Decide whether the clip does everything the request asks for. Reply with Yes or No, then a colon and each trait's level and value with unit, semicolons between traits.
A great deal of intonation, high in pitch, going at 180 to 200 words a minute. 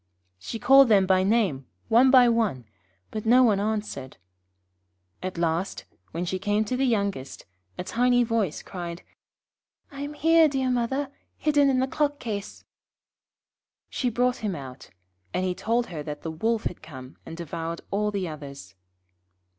No: wide, 6.5 semitones; high, 210 Hz; average, 160 wpm